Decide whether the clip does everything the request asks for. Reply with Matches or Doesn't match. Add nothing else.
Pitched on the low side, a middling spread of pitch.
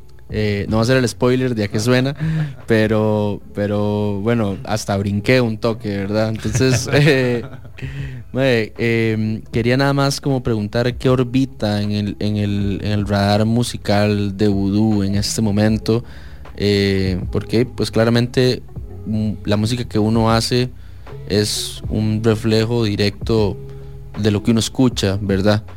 Matches